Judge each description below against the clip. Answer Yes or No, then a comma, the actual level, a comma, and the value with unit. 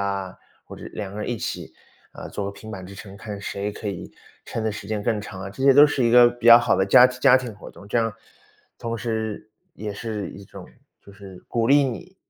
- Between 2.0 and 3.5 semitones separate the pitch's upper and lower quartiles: Yes, average, 3.2 semitones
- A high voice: No, low, 110 Hz